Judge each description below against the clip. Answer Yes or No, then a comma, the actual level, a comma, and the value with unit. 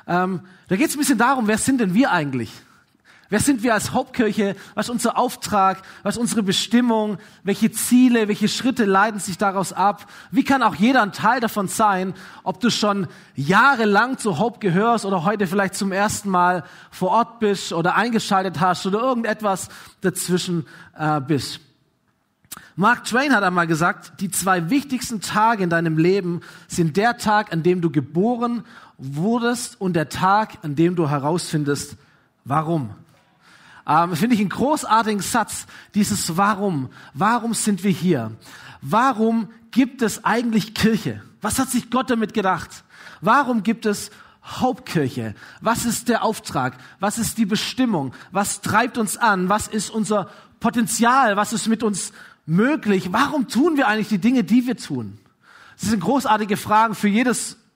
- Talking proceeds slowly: No, average, 160 wpm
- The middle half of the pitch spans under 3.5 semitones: No, average, 4.0 semitones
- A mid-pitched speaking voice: No, high, 205 Hz